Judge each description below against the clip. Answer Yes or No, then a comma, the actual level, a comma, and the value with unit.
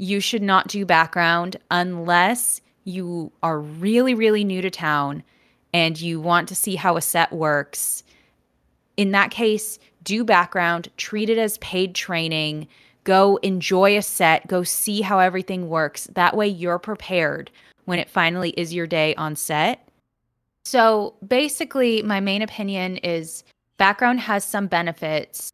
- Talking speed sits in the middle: Yes, average, 150 wpm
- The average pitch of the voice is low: No, medium, 185 Hz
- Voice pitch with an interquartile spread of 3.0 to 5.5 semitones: Yes, average, 3.7 semitones